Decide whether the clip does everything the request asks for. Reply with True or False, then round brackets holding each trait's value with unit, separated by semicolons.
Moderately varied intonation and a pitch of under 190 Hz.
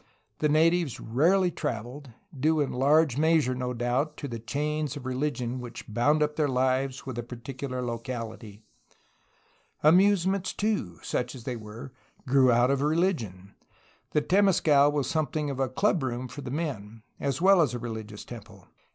True (4.1 semitones; 135 Hz)